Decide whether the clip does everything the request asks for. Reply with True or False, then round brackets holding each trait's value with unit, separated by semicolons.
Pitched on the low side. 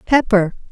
False (210 Hz)